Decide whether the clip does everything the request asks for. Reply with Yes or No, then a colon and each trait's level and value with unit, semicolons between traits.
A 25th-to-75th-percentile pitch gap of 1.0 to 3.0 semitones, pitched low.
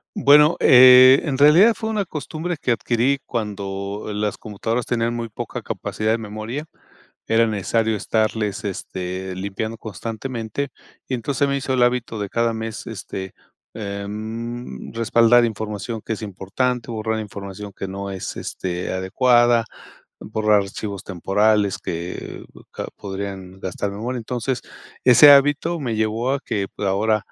No: average, 3.5 semitones; low, 110 Hz